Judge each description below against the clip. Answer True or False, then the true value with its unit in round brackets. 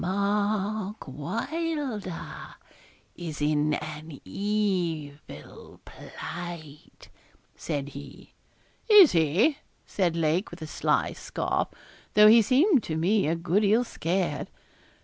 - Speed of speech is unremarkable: False (105 wpm)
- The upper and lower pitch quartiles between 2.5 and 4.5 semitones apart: False (5.3 semitones)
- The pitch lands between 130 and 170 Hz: False (180 Hz)